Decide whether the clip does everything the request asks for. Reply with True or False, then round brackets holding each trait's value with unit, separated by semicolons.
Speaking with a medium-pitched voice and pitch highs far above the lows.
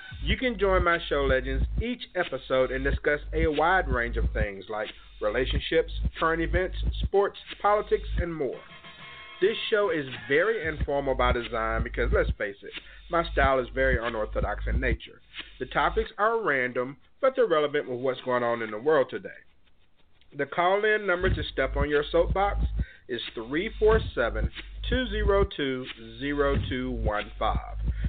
True (145 Hz; 7.6 semitones)